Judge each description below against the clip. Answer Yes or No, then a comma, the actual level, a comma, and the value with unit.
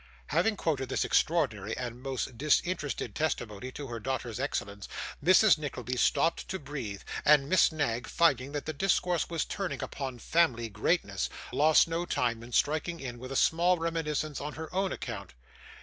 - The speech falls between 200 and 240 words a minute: No, average, 165 wpm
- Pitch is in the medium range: Yes, medium, 145 Hz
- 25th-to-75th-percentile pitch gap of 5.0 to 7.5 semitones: Yes, wide, 5.4 semitones